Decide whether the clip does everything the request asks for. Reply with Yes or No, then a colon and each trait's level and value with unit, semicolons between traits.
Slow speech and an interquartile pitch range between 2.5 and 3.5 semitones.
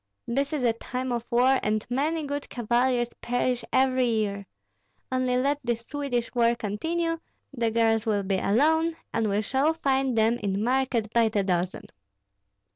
No: average, 160 wpm; average, 3.2 semitones